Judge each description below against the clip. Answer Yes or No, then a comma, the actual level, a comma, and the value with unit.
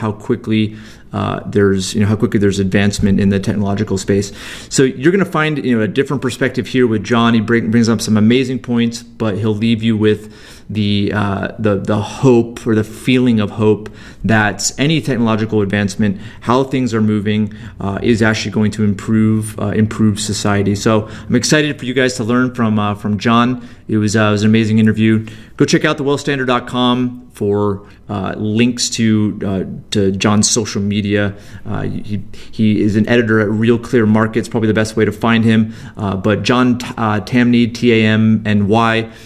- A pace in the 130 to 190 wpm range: No, average, 200 wpm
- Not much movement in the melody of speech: Yes, narrow, 2.3 semitones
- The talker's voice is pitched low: Yes, low, 110 Hz